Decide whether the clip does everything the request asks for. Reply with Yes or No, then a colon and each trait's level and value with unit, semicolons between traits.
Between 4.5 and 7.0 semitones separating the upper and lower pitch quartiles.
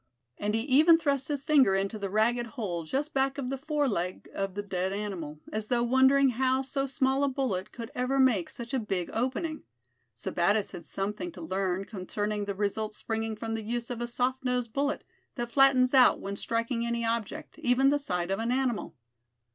Yes: average, 4.8 semitones